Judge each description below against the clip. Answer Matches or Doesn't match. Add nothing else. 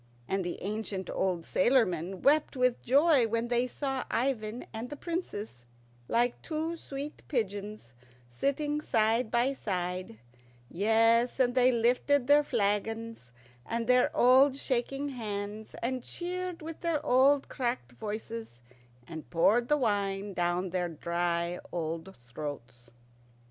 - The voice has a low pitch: Doesn't match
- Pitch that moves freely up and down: Matches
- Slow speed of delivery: Matches